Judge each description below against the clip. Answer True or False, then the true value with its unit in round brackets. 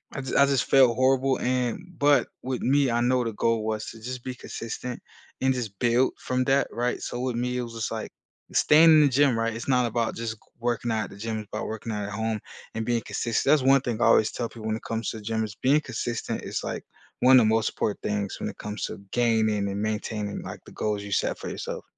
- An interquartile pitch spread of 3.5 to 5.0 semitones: False (2.8 semitones)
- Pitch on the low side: True (115 Hz)